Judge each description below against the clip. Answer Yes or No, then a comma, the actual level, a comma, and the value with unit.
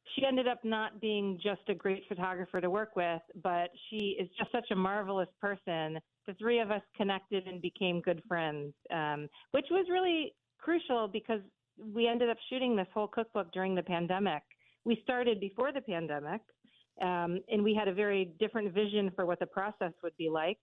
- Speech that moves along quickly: No, average, 190 wpm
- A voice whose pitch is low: No, high, 200 Hz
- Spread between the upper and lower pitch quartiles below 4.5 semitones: Yes, average, 3.4 semitones